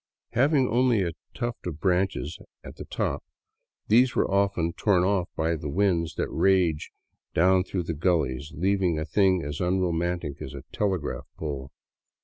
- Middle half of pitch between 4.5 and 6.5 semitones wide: No, average, 3.6 semitones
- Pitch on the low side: Yes, very low, 90 Hz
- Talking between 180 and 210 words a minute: No, average, 155 wpm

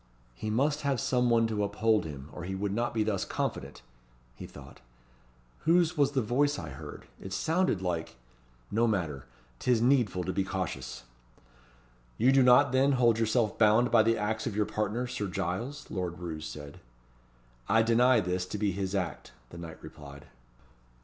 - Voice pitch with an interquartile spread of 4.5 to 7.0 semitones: Yes, average, 5.2 semitones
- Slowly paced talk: No, average, 175 wpm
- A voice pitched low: Yes, low, 110 Hz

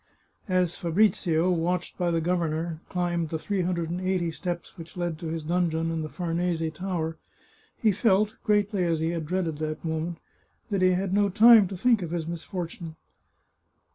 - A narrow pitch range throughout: Yes, narrow, 2.2 semitones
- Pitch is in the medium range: Yes, medium, 175 Hz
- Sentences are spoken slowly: No, average, 175 wpm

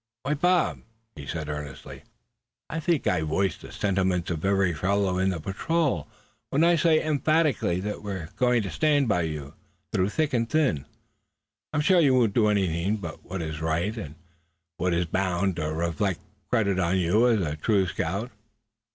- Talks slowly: No, average, 175 wpm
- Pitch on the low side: Yes, very low, 95 Hz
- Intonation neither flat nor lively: No, wide, 6.5 semitones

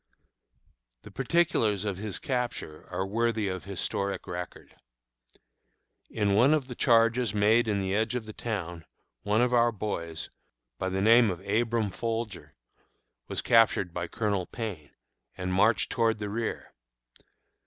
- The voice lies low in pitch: Yes, low, 105 Hz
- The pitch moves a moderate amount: Yes, average, 3.4 semitones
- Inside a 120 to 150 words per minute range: Yes, average, 145 wpm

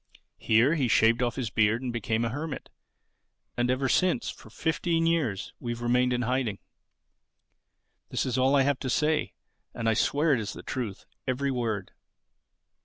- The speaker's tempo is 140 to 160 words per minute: No, average, 170 wpm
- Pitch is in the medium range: No, low, 125 Hz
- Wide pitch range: No, average, 3.3 semitones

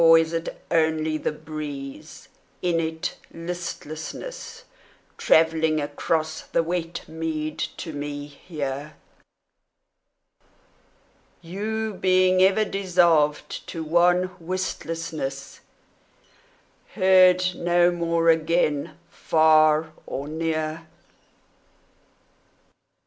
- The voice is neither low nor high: Yes, medium, 165 Hz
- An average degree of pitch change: No, narrow, 2.2 semitones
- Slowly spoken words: Yes, slow, 80 wpm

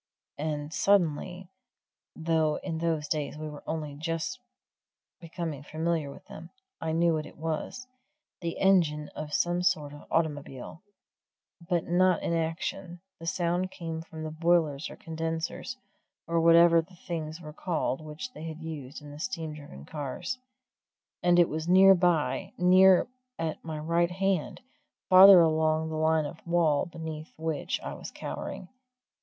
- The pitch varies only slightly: Yes, narrow, 2.1 semitones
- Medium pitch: Yes, medium, 165 Hz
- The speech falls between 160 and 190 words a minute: No, average, 150 wpm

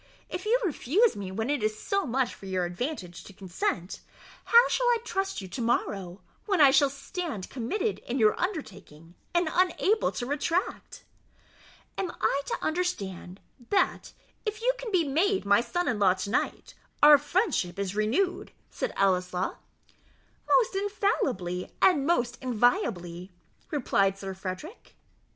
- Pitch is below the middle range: No, very high, 260 Hz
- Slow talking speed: No, average, 150 wpm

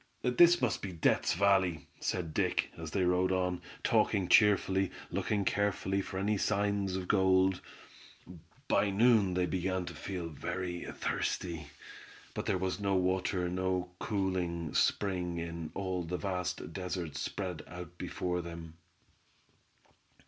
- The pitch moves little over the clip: Yes, narrow, 1.8 semitones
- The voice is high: No, very low, 95 Hz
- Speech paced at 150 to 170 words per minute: No, slow, 135 wpm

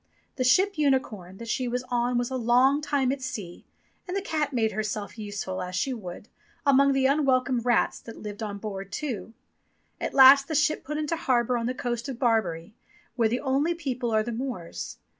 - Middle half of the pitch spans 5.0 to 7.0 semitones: No, average, 4.1 semitones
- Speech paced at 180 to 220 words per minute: Yes, average, 195 wpm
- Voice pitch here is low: No, high, 245 Hz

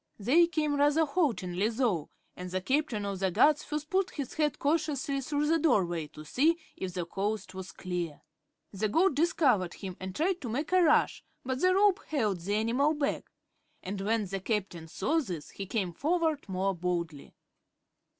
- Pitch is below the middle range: No, high, 230 Hz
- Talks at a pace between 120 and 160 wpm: No, average, 180 wpm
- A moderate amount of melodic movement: No, wide, 8.4 semitones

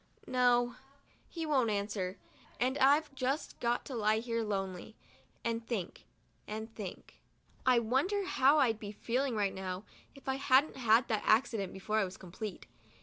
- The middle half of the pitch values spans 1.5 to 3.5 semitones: No, average, 3.9 semitones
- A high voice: Yes, high, 230 Hz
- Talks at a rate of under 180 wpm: Yes, average, 155 wpm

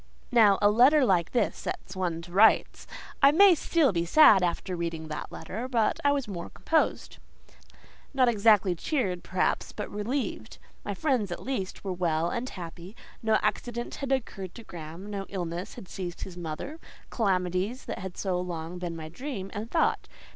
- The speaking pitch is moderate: No, high, 195 Hz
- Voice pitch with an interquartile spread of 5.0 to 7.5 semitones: Yes, wide, 5.5 semitones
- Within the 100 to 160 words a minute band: No, average, 170 wpm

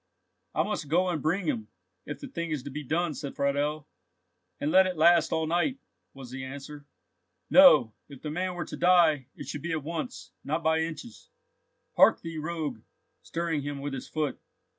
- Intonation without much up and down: No, average, 3.2 semitones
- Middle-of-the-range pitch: Yes, medium, 155 Hz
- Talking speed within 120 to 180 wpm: No, average, 190 wpm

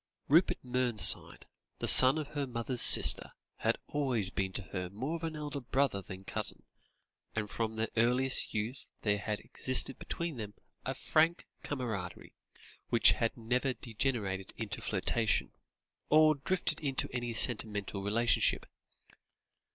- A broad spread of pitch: No, average, 4.4 semitones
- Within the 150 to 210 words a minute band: No, slow, 135 wpm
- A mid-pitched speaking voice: No, low, 120 Hz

